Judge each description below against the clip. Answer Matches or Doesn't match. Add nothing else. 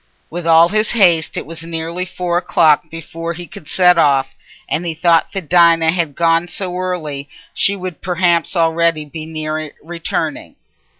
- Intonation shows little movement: Matches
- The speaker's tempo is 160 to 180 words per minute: Matches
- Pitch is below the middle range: Doesn't match